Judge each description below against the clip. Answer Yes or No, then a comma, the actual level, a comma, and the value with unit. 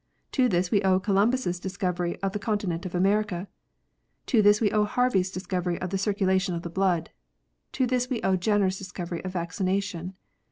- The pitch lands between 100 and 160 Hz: No, high, 190 Hz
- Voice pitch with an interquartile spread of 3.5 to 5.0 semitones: No, narrow, 2.4 semitones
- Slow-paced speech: No, average, 190 wpm